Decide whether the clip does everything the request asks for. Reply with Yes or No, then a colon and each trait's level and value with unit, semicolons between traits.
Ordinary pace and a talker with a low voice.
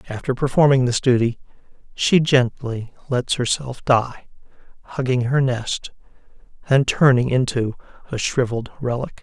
No: slow, 115 wpm; low, 125 Hz